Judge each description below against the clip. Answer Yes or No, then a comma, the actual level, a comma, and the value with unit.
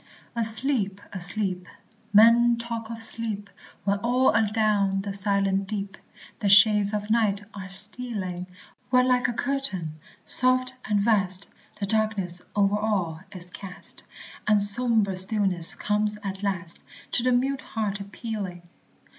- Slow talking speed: Yes, slow, 130 wpm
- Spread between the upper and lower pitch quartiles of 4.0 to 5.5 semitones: No, average, 2.8 semitones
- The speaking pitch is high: Yes, high, 205 Hz